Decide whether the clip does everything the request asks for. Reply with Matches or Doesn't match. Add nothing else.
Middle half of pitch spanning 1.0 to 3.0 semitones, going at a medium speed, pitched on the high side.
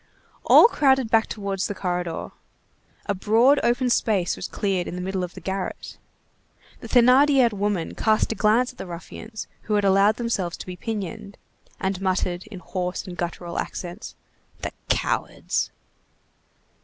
Doesn't match